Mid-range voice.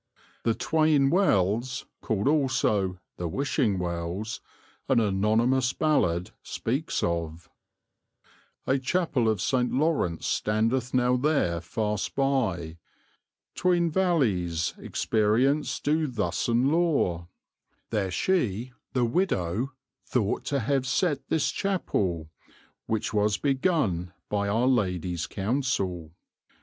No: low, 115 Hz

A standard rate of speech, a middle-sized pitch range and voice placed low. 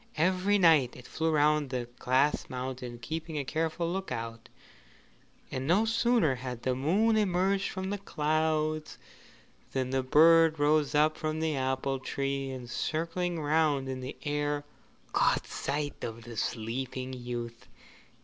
No: average, 145 wpm; average, 3.9 semitones; medium, 150 Hz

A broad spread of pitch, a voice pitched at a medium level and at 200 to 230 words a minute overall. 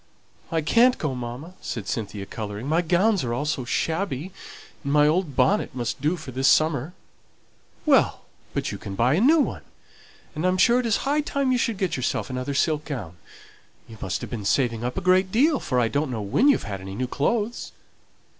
Yes: wide, 7.6 semitones; medium, 150 Hz; fast, 205 wpm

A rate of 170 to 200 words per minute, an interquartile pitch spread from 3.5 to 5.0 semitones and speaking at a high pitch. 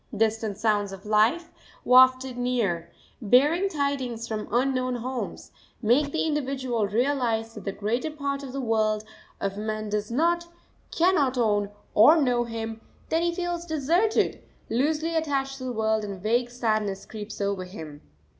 No: average, 155 wpm; average, 4.6 semitones; high, 245 Hz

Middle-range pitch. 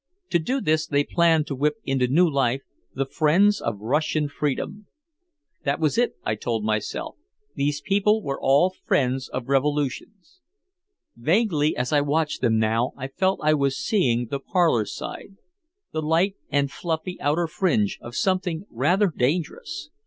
Yes: medium, 150 Hz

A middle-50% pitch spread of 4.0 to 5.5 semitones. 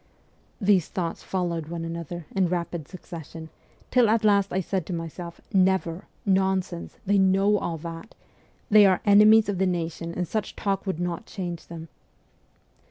No: average, 2.7 semitones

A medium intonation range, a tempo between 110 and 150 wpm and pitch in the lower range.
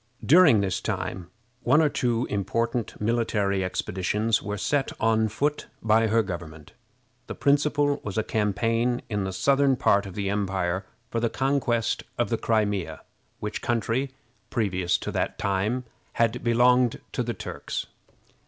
Yes: average, 3.8 semitones; average, 145 wpm; low, 110 Hz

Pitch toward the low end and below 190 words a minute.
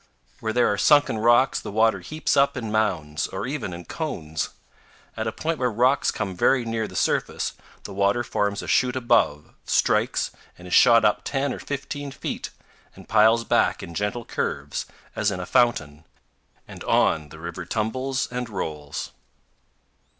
Yes: low, 110 Hz; average, 170 wpm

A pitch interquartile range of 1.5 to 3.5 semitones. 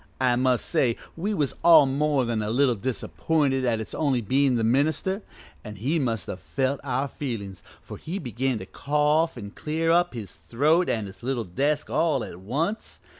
No: average, 4.8 semitones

